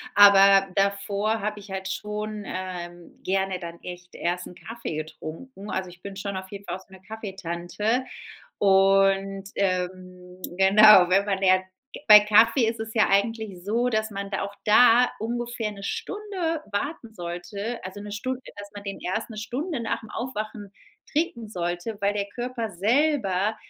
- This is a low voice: No, high, 200 Hz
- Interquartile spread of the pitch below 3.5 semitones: Yes, average, 2.8 semitones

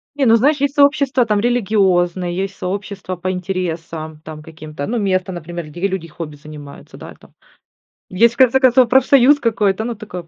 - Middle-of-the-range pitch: No, high, 195 Hz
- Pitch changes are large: Yes, wide, 5.7 semitones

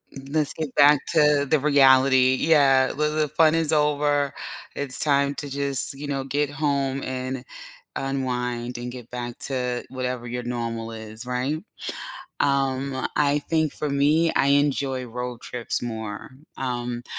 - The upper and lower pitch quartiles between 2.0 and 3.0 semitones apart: Yes, narrow, 2.6 semitones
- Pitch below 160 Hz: Yes, low, 135 Hz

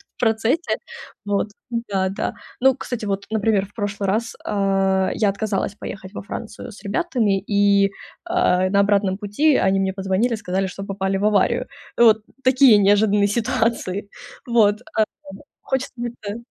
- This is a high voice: Yes, high, 205 Hz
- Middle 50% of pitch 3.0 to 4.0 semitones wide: No, narrow, 2.4 semitones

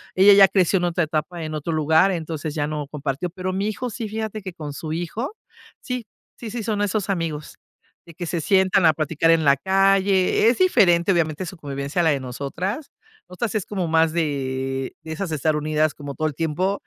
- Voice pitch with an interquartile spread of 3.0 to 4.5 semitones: Yes, average, 4.1 semitones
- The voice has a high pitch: No, medium, 170 Hz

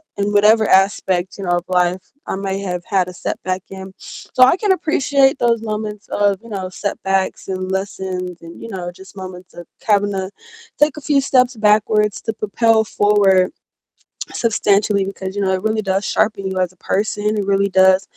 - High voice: Yes, high, 200 Hz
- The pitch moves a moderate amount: No, narrow, 2.3 semitones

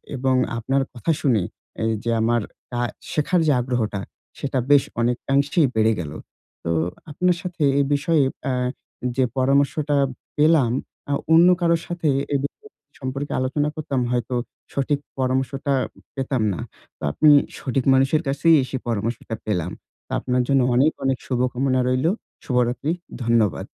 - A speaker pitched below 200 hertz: Yes, low, 135 Hz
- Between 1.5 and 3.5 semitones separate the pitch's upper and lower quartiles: Yes, average, 2.8 semitones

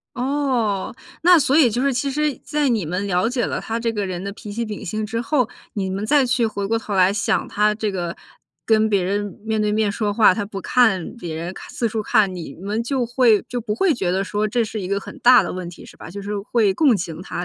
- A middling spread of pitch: Yes, average, 3.6 semitones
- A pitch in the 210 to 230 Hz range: Yes, high, 215 Hz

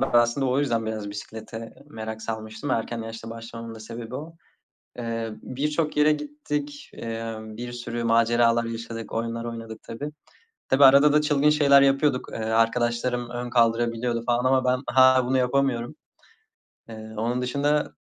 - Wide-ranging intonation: No, average, 2.9 semitones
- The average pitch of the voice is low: Yes, low, 120 Hz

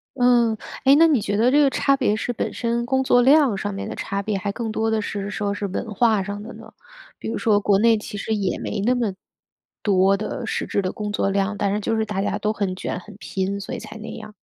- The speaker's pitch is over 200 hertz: Yes, high, 215 Hz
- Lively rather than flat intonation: No, average, 2.8 semitones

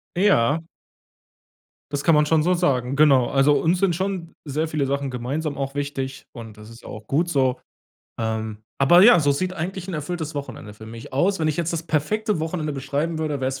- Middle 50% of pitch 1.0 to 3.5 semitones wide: No, average, 3.9 semitones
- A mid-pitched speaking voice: Yes, medium, 145 Hz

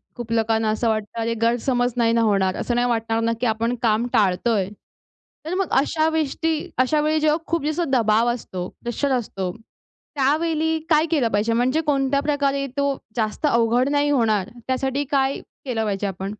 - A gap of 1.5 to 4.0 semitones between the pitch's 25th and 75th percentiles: No, average, 4.4 semitones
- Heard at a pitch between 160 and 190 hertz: No, high, 245 Hz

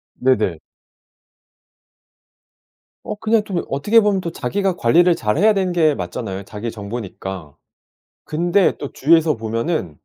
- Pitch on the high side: No, medium, 145 Hz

